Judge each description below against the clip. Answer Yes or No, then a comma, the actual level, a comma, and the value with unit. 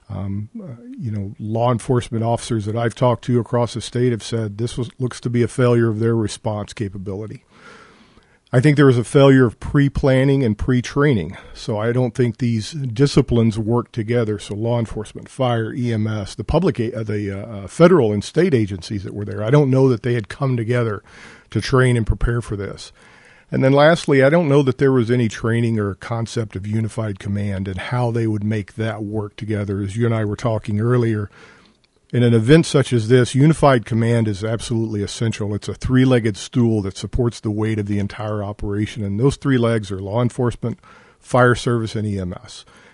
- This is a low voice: Yes, low, 115 Hz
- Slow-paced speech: No, average, 200 wpm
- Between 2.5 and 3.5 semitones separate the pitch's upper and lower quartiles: Yes, average, 2.9 semitones